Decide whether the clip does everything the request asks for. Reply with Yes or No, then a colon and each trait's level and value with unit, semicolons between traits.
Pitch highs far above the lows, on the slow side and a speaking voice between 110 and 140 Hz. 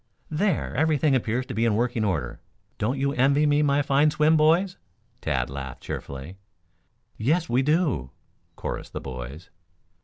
No: wide, 6.7 semitones; average, 150 wpm; low, 135 Hz